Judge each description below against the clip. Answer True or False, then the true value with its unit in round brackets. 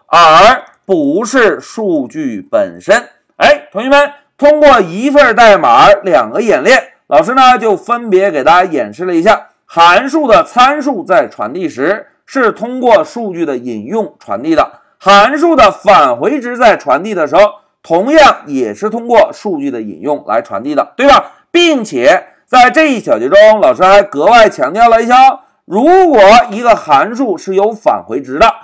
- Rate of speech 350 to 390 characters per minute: False (240 characters per minute)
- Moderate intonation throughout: False (6.5 semitones)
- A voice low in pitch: False (265 Hz)